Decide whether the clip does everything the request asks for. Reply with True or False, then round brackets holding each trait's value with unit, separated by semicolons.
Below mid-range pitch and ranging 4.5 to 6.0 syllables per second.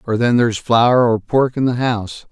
True (120 Hz; 5.1 syllables/s)